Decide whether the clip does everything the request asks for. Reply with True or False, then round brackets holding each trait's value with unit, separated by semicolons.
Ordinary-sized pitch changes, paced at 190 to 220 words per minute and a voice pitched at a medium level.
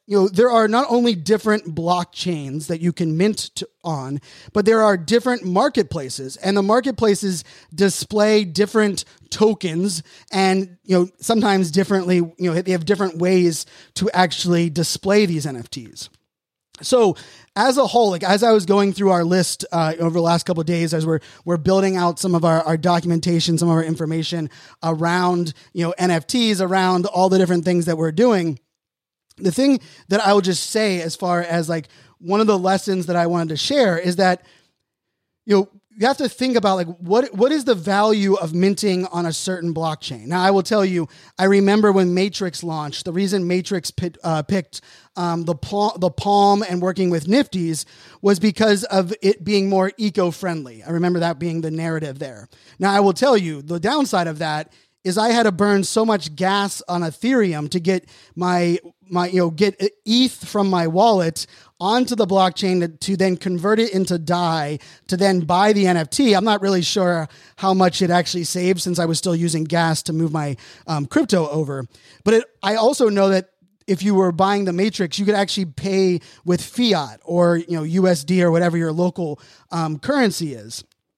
True (3.1 semitones; 195 wpm; 180 Hz)